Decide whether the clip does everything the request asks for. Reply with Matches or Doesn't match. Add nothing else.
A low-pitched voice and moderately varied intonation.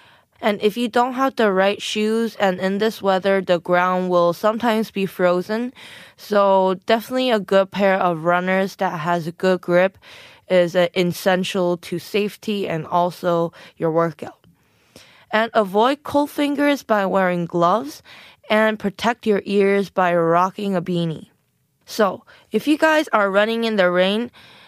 Doesn't match